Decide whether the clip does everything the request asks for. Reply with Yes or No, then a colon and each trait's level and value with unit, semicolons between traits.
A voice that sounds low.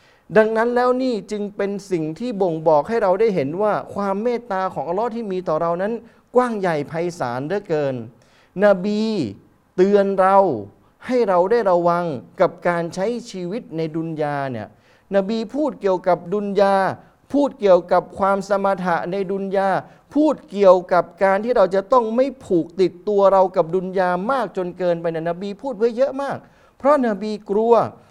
No: high, 195 Hz